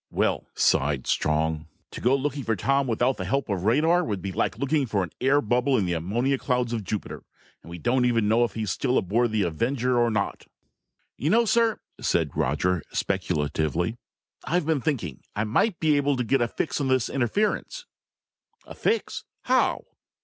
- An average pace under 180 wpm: No, average, 185 wpm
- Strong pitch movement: Yes, wide, 6.0 semitones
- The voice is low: Yes, low, 120 Hz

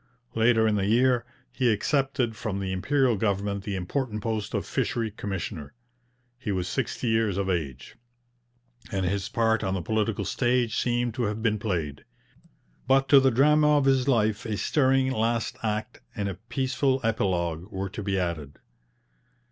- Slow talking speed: No, average, 165 wpm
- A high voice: No, low, 110 Hz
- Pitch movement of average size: Yes, average, 4.2 semitones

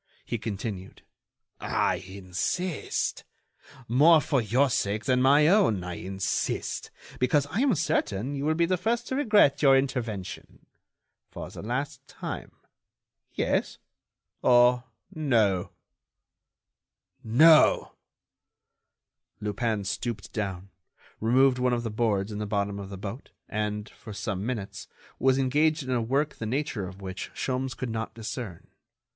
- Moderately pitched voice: No, low, 120 Hz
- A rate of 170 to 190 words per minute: No, slow, 135 wpm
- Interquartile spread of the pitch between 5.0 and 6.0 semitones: Yes, wide, 5.5 semitones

